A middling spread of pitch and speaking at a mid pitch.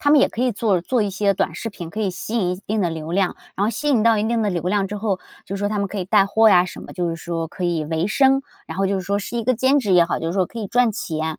No: average, 4.0 semitones; high, 200 Hz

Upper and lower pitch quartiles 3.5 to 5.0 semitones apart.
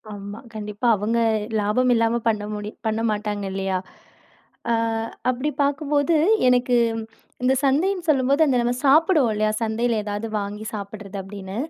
Yes: average, 4.2 semitones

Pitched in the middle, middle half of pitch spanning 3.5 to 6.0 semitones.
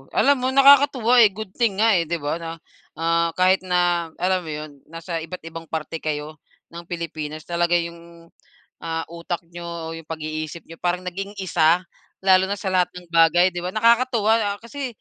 No: medium, 175 Hz; average, 2.9 semitones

